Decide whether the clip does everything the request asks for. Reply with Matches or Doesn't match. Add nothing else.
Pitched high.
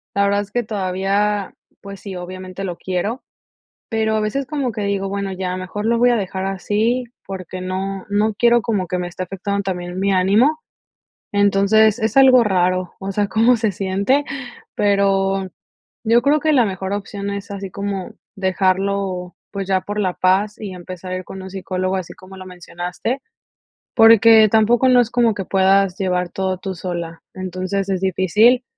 Matches